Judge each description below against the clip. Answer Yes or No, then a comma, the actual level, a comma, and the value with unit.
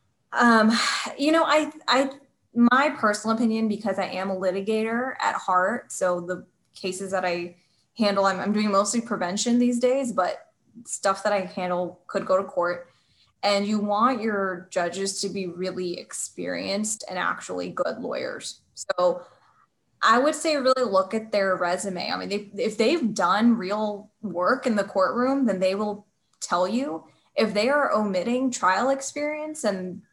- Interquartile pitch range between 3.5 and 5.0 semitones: Yes, average, 4.3 semitones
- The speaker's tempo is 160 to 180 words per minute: Yes, average, 165 wpm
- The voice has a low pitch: No, high, 205 Hz